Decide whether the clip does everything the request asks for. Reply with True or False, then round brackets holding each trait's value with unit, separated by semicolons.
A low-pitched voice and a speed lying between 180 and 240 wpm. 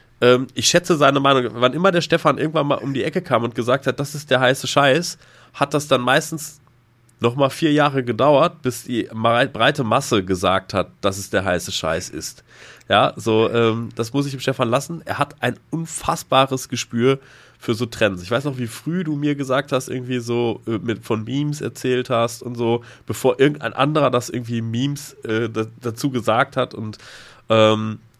True (125 Hz; 190 wpm)